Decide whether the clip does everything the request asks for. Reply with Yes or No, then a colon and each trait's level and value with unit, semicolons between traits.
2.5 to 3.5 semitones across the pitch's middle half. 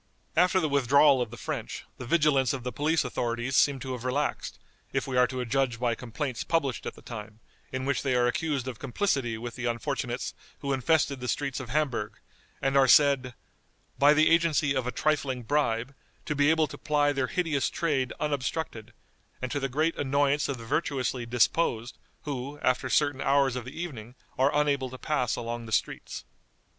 Yes: average, 2.9 semitones